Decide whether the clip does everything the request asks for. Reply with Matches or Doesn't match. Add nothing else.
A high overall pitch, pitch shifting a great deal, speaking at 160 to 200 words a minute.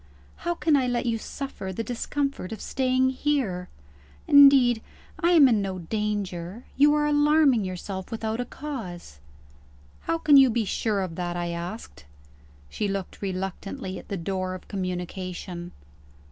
Doesn't match